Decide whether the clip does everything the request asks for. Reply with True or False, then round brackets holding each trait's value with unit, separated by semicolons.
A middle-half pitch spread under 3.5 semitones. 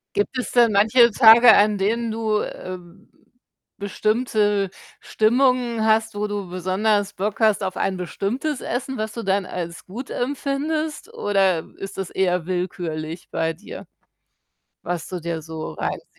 False (4.1 semitones)